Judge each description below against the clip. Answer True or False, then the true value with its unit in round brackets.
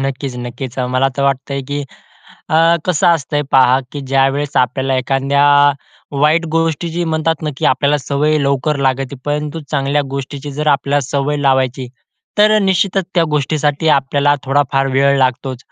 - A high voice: False (140 Hz)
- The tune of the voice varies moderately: False (2.0 semitones)